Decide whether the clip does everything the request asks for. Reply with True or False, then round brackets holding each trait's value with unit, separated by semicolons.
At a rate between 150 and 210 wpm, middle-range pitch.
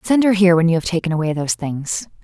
False (270 wpm; 175 Hz)